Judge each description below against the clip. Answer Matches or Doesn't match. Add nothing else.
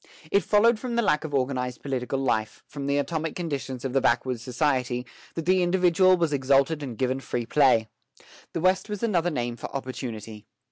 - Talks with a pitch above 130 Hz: Matches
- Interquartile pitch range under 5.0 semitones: Doesn't match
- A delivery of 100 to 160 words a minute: Doesn't match